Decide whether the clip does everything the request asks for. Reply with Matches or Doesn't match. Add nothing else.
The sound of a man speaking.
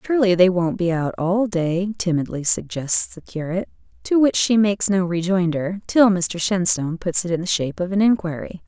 Doesn't match